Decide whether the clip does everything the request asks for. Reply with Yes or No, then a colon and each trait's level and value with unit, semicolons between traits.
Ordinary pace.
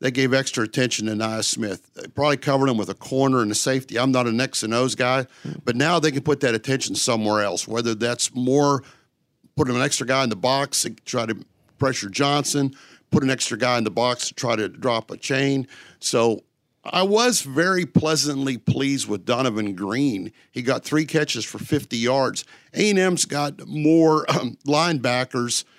Yes: average, 195 wpm